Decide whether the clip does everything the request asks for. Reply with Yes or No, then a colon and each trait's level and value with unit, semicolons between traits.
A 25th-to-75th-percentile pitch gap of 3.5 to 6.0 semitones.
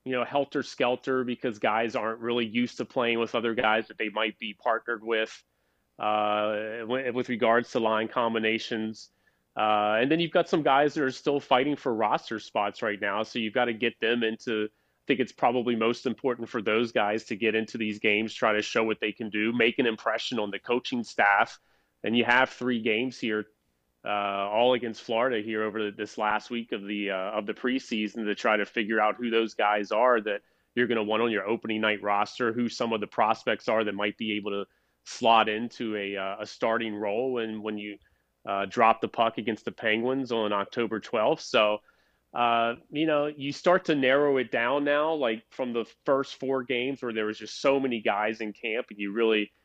No: narrow, 2.5 semitones